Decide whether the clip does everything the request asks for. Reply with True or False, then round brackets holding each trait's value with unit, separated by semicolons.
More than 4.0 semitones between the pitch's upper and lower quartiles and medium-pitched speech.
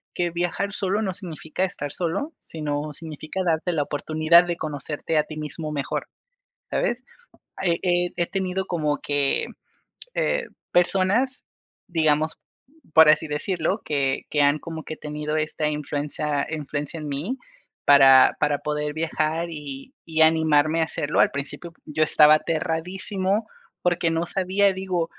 False (2.9 semitones; 160 Hz)